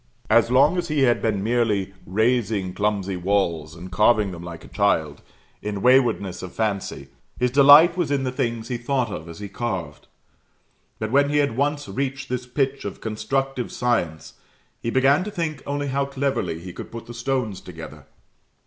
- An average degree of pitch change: No, wide, 5.7 semitones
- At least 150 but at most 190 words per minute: Yes, average, 180 wpm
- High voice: No, low, 120 Hz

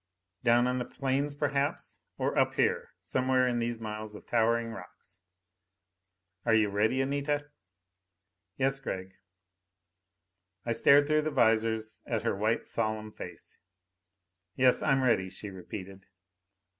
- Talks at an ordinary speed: No, slow, 130 wpm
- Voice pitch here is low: Yes, low, 120 Hz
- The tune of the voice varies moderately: Yes, average, 3.9 semitones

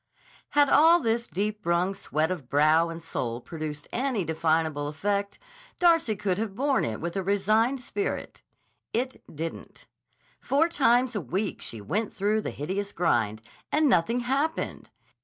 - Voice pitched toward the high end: Yes, high, 200 Hz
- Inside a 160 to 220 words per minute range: No, average, 150 wpm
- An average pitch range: No, wide, 7.2 semitones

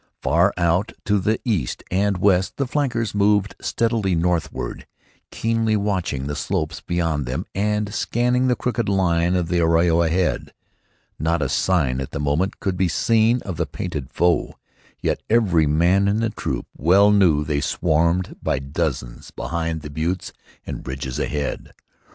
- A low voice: Yes, very low, 90 Hz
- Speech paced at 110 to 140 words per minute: No, average, 155 wpm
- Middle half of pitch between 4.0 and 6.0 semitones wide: Yes, average, 4.7 semitones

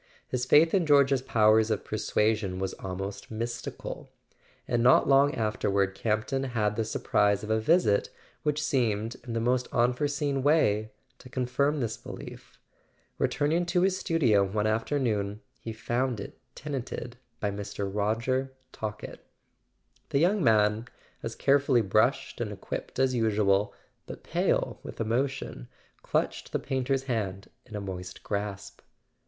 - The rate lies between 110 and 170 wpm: Yes, average, 140 wpm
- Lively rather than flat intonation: No, average, 4.3 semitones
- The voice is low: Yes, low, 115 Hz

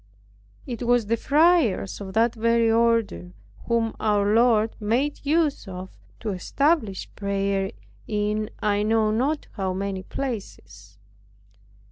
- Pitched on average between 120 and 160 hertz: No, high, 220 Hz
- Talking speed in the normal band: No, slow, 120 wpm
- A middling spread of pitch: Yes, average, 3.0 semitones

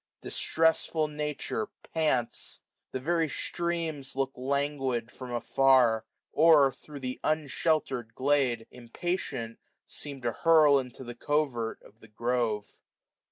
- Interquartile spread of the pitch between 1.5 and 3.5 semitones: No, average, 4.1 semitones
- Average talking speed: No, slow, 115 wpm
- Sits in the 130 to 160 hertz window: Yes, low, 135 Hz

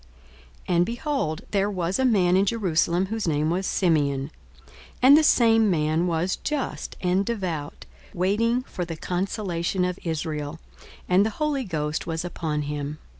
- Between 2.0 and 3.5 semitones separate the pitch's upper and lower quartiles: No, average, 4.8 semitones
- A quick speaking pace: No, average, 155 wpm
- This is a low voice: No, medium, 180 Hz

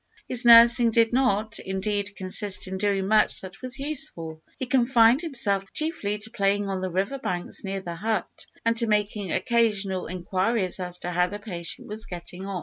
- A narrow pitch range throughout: No, average, 3.5 semitones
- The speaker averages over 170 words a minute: Yes, average, 180 wpm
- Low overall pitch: No, high, 205 Hz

